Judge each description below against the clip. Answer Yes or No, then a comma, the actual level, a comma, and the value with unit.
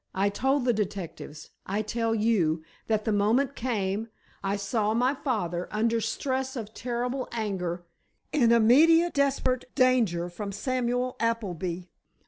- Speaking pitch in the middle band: No, high, 225 Hz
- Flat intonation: No, average, 4.2 semitones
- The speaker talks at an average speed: No, slow, 115 wpm